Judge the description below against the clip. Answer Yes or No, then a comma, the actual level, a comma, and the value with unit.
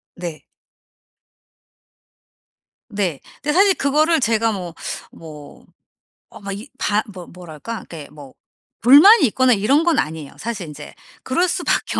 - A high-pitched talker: Yes, high, 210 Hz